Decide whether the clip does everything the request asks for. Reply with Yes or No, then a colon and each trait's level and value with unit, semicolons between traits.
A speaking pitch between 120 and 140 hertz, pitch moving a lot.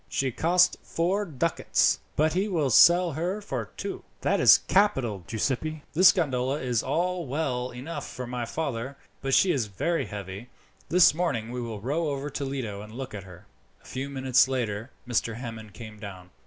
Yes: low, 135 Hz; wide, 5.9 semitones